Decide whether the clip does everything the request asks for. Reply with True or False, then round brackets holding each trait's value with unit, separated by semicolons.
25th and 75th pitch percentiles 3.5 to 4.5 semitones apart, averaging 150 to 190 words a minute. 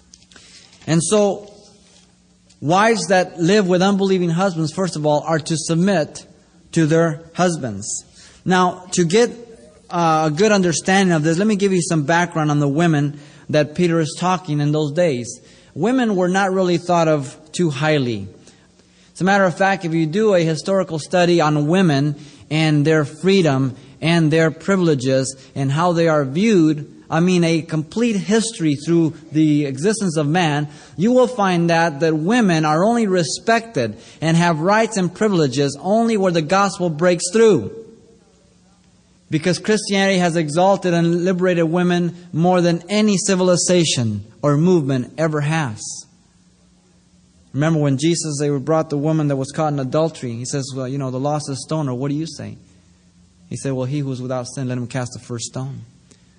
True (4.0 semitones; 170 wpm)